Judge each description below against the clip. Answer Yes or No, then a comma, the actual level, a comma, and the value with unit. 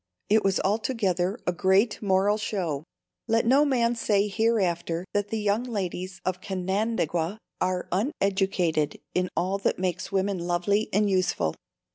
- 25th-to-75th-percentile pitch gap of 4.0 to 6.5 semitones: No, average, 2.8 semitones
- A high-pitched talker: Yes, high, 195 Hz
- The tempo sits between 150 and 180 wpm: No, average, 140 wpm